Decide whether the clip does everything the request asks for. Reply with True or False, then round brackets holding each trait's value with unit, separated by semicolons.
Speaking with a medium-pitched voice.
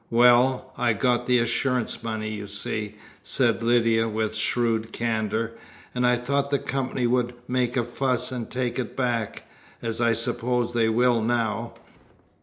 False (120 Hz)